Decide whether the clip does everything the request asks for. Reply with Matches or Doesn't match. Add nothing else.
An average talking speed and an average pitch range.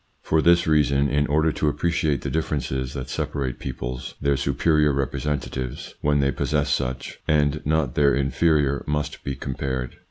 Doesn't match